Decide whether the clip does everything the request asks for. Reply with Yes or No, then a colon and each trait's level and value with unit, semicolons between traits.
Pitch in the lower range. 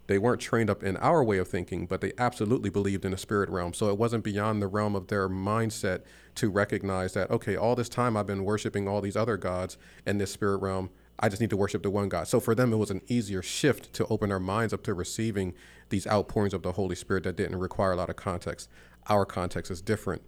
Yes: low, 100 Hz